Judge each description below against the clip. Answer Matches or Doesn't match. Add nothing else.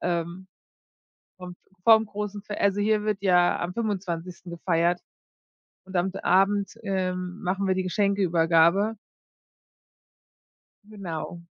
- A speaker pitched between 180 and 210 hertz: Matches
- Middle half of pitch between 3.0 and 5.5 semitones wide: Doesn't match